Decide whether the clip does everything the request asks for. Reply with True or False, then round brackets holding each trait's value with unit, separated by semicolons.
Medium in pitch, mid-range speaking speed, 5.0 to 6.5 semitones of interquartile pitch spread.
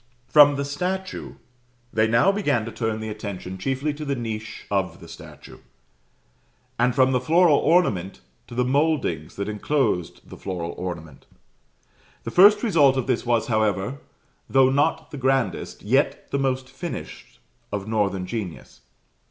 False (125 Hz; 150 wpm; 5.5 semitones)